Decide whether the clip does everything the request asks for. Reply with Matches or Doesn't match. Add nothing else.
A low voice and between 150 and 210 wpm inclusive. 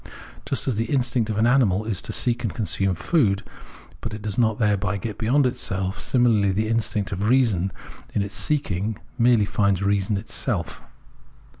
Matches